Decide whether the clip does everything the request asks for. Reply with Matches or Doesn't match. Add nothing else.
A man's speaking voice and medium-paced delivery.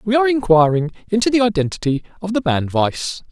Matches